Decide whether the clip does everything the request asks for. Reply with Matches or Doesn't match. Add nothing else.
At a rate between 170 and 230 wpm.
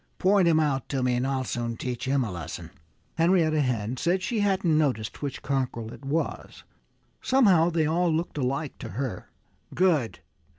Matches